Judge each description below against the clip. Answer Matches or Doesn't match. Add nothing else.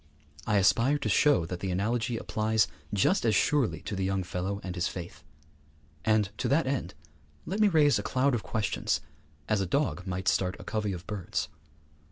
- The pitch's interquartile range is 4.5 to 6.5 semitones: Matches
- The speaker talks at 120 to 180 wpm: Doesn't match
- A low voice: Matches